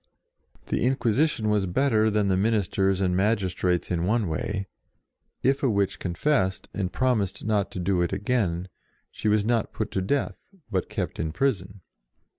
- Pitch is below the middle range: Yes, low, 100 Hz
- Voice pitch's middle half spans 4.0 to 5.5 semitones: No, average, 3.4 semitones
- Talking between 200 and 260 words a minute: No, average, 170 wpm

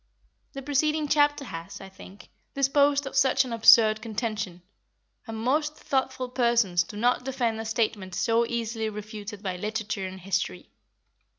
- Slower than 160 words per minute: Yes, average, 150 wpm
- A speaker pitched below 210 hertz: No, high, 225 Hz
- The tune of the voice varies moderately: Yes, average, 4.3 semitones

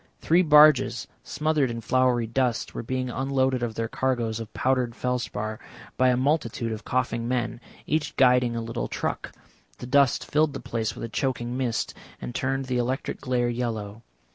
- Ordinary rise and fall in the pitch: No, narrow, 2.2 semitones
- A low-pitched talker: Yes, low, 125 Hz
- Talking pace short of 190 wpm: Yes, average, 170 wpm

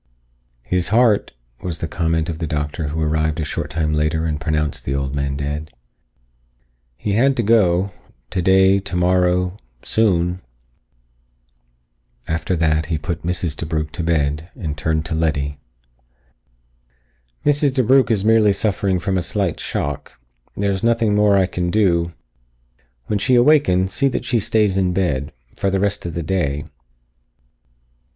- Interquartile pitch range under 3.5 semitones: No, average, 4.4 semitones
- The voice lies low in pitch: Yes, very low, 90 Hz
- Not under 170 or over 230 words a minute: No, average, 150 wpm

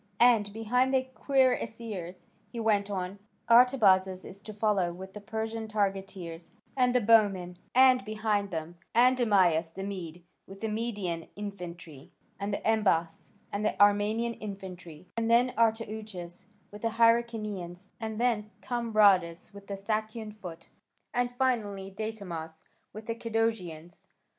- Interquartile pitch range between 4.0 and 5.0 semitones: No, average, 3.5 semitones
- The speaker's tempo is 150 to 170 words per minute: No, slow, 135 wpm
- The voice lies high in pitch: Yes, high, 210 Hz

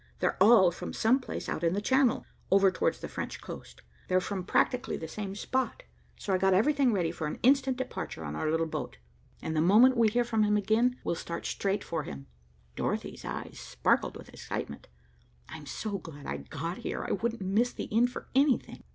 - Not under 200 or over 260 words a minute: Yes, fast, 205 wpm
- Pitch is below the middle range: No, high, 200 Hz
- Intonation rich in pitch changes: Yes, wide, 6.4 semitones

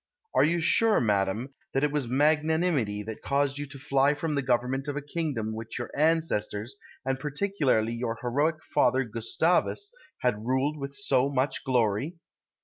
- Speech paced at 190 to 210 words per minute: No, average, 155 wpm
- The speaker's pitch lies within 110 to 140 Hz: Yes, low, 135 Hz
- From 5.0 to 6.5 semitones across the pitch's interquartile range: No, average, 3.9 semitones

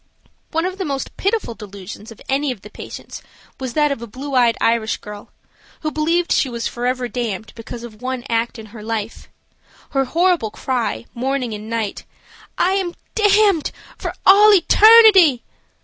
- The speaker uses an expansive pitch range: Yes, wide, 6.8 semitones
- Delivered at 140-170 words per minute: Yes, average, 165 wpm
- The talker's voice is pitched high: Yes, very high, 255 Hz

